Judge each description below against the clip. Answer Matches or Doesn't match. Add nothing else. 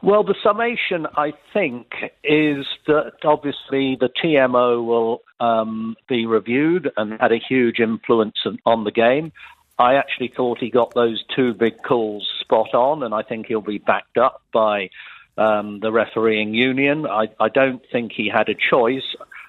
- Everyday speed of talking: Matches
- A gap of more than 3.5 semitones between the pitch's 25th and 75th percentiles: Matches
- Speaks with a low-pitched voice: Matches